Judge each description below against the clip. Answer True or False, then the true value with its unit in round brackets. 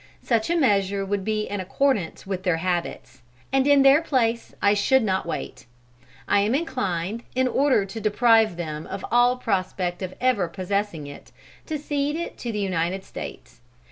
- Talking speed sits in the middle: True (170 wpm)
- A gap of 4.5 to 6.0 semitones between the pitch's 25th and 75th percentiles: True (5.5 semitones)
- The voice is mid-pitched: False (205 Hz)